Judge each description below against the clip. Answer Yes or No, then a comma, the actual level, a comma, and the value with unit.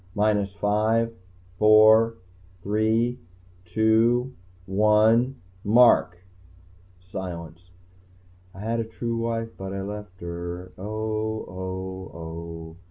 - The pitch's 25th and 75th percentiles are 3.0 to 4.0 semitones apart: Yes, average, 3.4 semitones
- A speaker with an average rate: No, slow, 95 wpm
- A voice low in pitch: Yes, low, 105 Hz